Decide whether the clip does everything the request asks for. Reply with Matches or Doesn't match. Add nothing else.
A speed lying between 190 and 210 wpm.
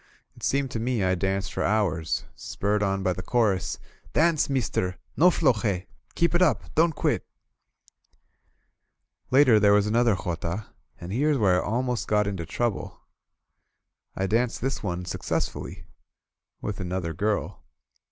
Doesn't match